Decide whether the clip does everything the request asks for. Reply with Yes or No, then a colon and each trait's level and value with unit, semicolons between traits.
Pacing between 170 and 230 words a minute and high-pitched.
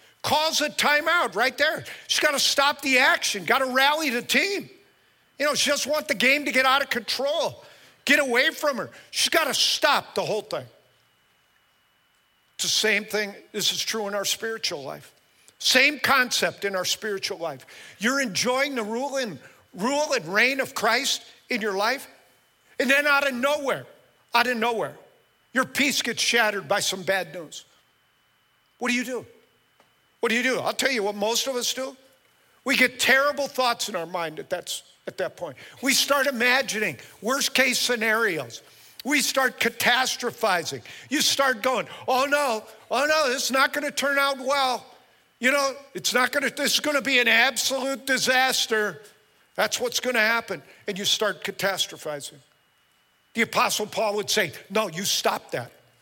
Yes: average, 180 wpm; very high, 250 Hz